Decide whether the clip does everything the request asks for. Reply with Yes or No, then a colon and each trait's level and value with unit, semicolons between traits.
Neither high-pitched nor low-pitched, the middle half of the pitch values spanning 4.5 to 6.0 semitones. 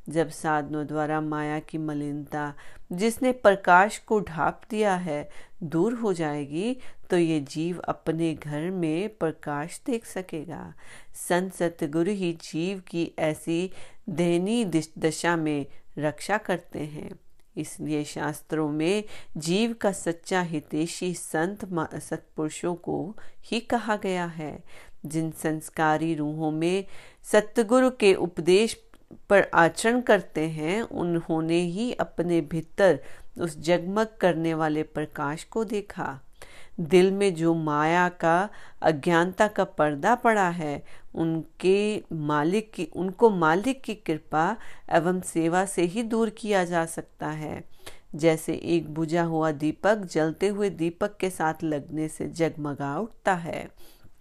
No: medium, 170 Hz; average, 3.9 semitones